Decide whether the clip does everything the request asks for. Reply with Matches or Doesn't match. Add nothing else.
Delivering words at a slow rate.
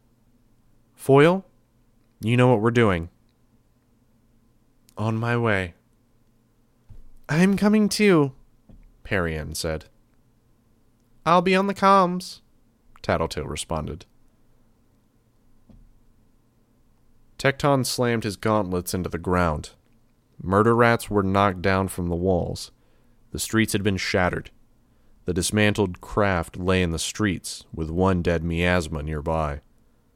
Matches